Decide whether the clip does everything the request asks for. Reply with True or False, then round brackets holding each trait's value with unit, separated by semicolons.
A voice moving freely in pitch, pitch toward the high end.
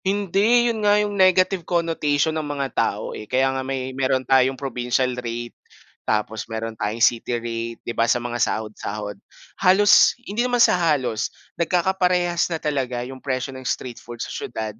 False (7.1 semitones; 135 Hz)